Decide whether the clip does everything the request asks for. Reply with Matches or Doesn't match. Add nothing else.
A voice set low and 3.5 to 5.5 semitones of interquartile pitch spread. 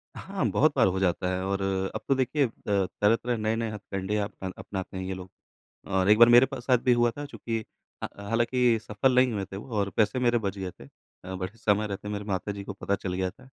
Matches